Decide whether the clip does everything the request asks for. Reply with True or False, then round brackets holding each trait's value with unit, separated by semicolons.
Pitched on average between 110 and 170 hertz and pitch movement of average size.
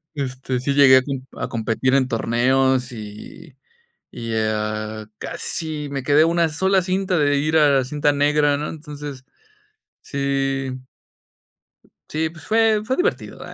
True (140 Hz; 3.2 semitones)